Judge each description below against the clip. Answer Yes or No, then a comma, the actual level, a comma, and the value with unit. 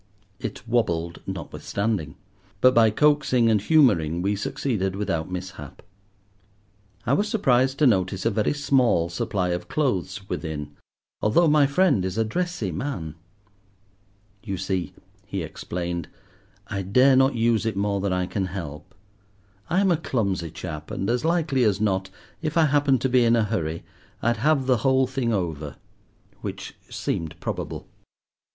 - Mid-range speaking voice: No, low, 105 Hz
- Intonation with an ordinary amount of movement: No, wide, 6.5 semitones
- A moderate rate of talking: Yes, average, 150 wpm